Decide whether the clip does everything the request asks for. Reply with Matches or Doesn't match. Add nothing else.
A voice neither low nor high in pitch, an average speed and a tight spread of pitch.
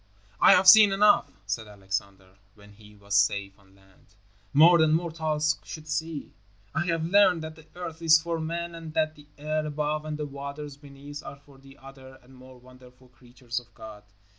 Doesn't match